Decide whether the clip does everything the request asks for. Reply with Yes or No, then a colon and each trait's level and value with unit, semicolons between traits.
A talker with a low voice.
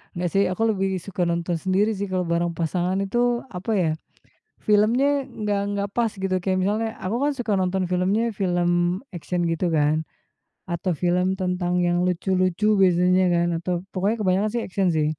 No: medium, 185 Hz